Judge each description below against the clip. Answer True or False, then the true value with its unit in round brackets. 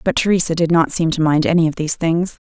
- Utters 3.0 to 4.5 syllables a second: False (6.5 syllables/s)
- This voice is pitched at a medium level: True (165 Hz)